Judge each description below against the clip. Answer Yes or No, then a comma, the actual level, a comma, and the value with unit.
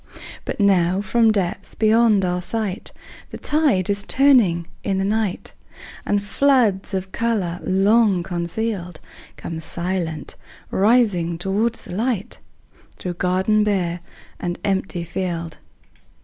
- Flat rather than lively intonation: No, average, 3.5 semitones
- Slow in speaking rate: Yes, slow, 120 wpm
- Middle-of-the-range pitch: No, high, 195 Hz